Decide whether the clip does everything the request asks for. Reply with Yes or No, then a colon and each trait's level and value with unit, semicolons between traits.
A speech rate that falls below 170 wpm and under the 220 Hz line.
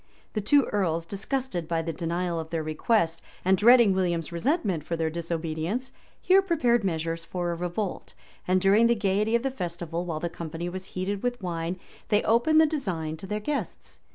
No: average, 185 wpm; medium, 185 Hz